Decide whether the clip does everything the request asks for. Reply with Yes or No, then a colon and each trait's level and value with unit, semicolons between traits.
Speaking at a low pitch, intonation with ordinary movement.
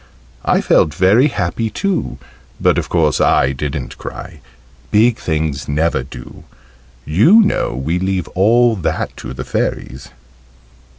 No: very low, 90 Hz; wide, 7.5 semitones